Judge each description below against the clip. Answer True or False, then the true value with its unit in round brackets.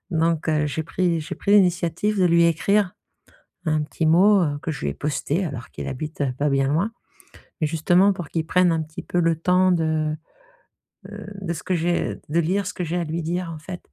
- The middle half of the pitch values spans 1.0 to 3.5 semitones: True (2.7 semitones)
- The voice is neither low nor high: True (165 Hz)